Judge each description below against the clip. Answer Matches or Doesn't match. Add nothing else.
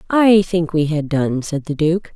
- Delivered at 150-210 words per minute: Doesn't match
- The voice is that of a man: Doesn't match